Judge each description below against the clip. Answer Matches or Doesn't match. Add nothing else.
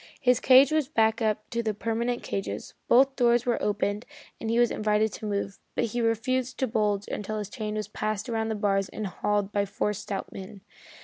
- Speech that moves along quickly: Matches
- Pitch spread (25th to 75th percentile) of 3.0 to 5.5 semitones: Doesn't match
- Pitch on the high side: Matches